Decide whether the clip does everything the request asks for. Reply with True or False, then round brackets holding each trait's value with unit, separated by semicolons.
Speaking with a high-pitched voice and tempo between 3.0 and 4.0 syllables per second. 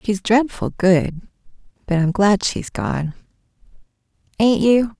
True (195 Hz; 3.6 syllables/s)